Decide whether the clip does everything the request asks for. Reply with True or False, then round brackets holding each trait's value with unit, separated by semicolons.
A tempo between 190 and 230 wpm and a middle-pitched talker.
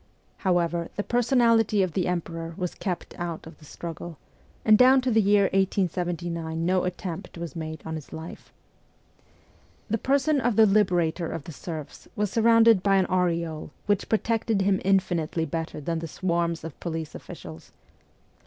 False (160 wpm; 180 Hz)